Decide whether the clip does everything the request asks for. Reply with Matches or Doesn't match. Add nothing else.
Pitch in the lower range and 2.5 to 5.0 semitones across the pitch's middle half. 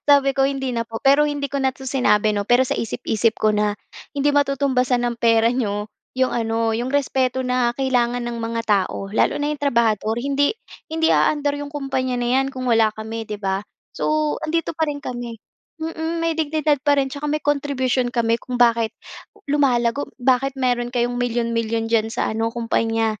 Doesn't match